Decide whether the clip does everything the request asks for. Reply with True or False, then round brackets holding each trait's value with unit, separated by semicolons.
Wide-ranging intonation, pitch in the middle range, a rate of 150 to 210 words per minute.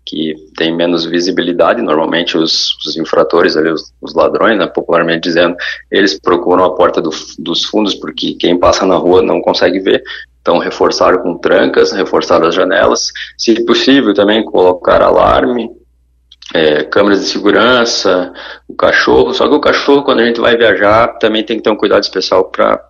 False (6.0 semitones; 95 Hz; 170 wpm)